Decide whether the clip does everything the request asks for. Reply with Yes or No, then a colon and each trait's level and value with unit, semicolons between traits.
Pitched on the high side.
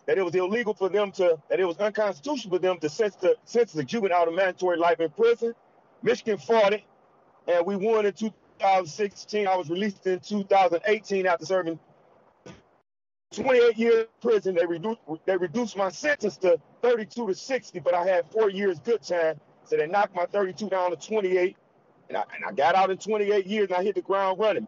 Yes: high, 200 Hz